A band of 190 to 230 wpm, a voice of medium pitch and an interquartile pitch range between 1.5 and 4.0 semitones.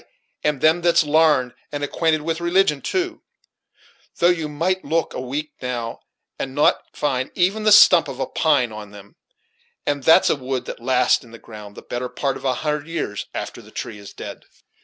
No: average, 195 wpm; medium, 145 Hz; average, 4.7 semitones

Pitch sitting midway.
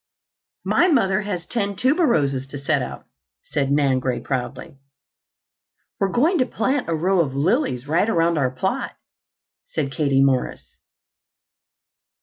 Yes: medium, 165 Hz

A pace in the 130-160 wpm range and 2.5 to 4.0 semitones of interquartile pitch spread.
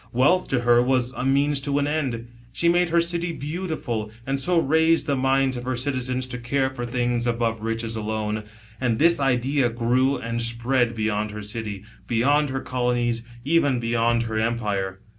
No: average, 180 wpm; average, 3.2 semitones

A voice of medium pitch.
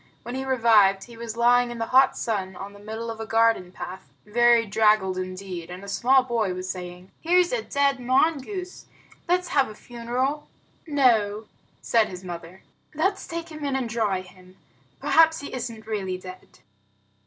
No: high, 230 Hz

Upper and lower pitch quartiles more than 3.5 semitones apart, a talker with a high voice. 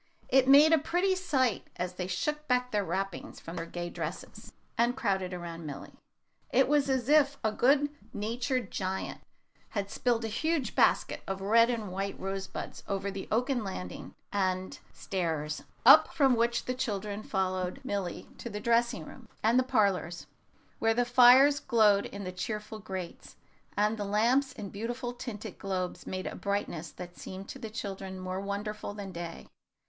Yes: average, 4.6 semitones; high, 210 Hz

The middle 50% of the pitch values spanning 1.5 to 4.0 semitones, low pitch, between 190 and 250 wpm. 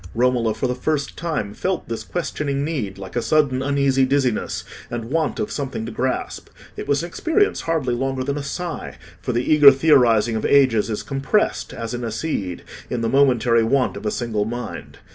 Yes: average, 3.7 semitones; low, 130 Hz; average, 195 wpm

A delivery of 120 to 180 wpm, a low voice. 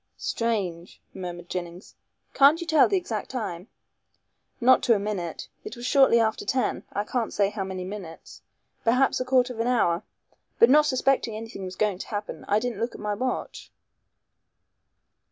No: average, 170 wpm; high, 220 Hz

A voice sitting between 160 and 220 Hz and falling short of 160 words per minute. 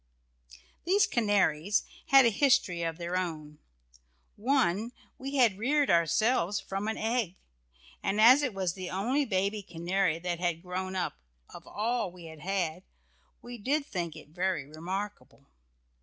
Yes: high, 190 Hz; average, 145 wpm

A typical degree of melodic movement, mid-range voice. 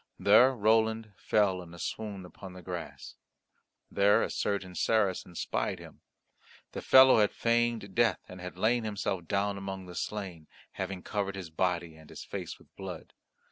No: average, 3.1 semitones; low, 100 Hz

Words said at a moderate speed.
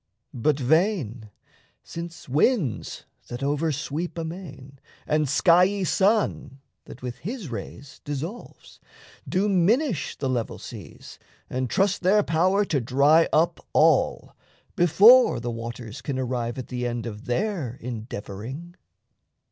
No: slow, 125 wpm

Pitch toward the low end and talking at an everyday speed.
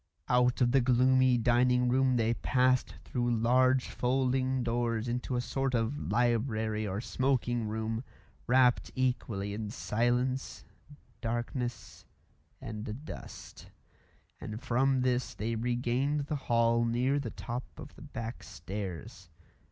No: low, 120 Hz; slow, 125 wpm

